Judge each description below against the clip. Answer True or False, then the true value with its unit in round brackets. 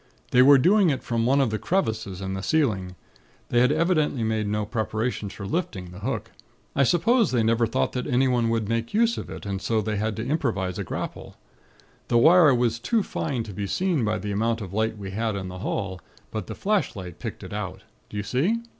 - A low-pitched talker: True (115 Hz)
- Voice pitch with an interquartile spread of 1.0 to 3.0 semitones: False (5.1 semitones)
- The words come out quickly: True (220 wpm)